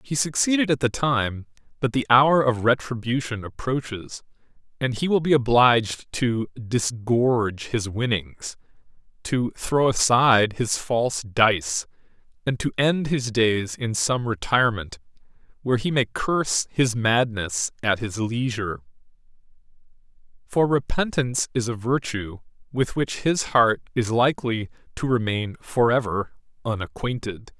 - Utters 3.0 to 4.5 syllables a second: Yes, 4.3 syllables/s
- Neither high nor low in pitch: No, low, 120 Hz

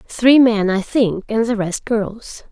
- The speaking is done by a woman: Yes, female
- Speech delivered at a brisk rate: No, average, 190 wpm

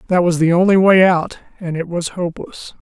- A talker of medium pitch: Yes, medium, 175 Hz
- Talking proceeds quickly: No, average, 190 wpm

